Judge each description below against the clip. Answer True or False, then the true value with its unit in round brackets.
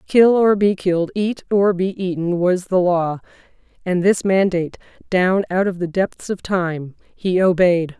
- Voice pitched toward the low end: False (185 Hz)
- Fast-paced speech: False (175 wpm)